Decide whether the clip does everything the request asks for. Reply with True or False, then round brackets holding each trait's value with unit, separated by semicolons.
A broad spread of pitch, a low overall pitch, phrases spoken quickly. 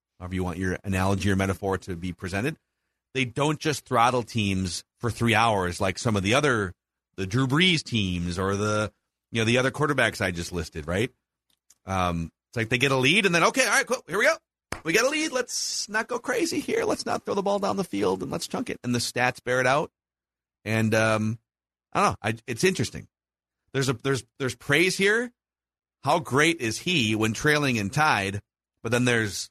True (7.5 semitones; 115 Hz; 215 wpm)